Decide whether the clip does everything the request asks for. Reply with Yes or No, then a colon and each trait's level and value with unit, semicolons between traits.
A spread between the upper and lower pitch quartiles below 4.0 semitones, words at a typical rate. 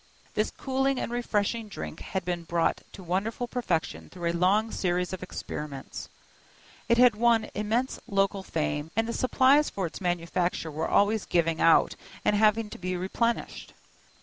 No: average, 4.7 semitones; average, 160 wpm